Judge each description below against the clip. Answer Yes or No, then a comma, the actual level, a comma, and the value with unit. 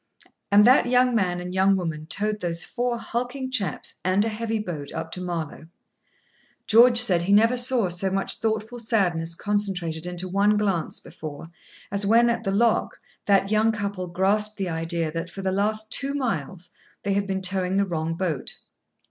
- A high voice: Yes, high, 195 Hz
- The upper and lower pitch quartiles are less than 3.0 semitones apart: No, average, 3.8 semitones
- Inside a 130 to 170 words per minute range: No, average, 180 wpm